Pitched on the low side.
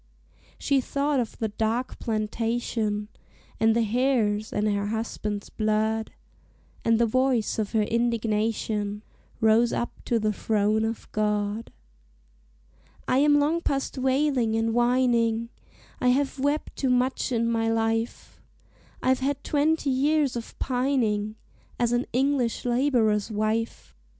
No: high, 230 Hz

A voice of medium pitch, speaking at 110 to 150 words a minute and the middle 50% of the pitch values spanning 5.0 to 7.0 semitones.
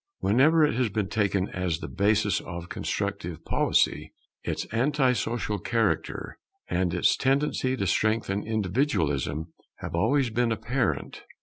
No: low, 110 Hz; slow, 135 wpm; average, 5.3 semitones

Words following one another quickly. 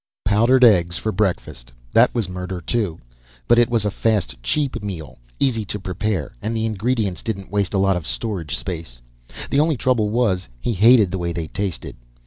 No: average, 185 wpm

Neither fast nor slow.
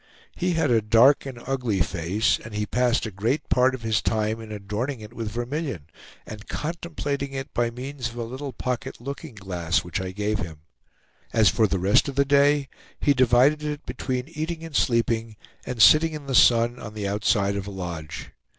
Yes: average, 195 wpm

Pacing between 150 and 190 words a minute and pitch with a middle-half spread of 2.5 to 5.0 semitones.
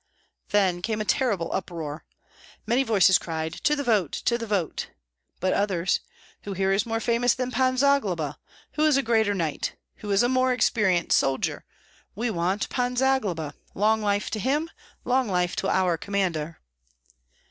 No: average, 165 wpm; wide, 5.5 semitones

